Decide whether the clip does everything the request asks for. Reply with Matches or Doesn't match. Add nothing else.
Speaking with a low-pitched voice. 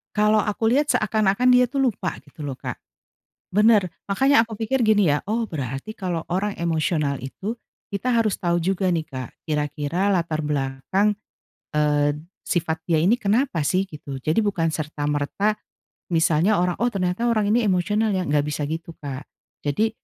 Doesn't match